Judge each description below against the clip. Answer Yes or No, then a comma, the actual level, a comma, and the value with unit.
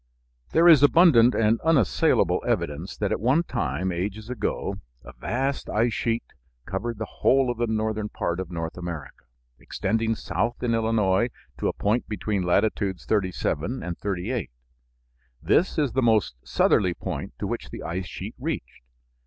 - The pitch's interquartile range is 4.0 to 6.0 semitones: Yes, average, 4.3 semitones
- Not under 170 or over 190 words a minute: No, average, 155 wpm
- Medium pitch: No, low, 110 Hz